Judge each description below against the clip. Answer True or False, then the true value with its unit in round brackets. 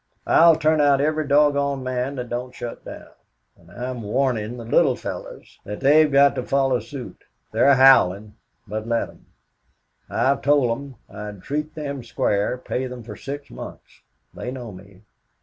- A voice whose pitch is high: False (130 Hz)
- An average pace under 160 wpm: False (165 wpm)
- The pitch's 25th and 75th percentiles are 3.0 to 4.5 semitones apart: True (3.4 semitones)